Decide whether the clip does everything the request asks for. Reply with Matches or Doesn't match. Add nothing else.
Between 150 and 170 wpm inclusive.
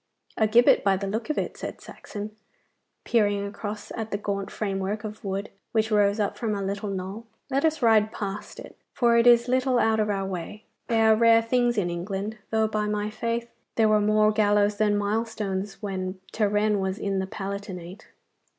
Doesn't match